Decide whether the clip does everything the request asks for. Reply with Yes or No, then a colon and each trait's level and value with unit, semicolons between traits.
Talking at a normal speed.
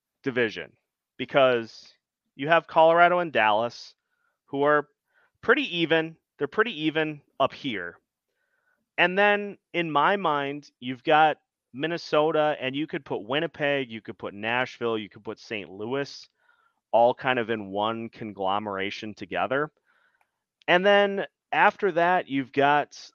No: slow, 130 wpm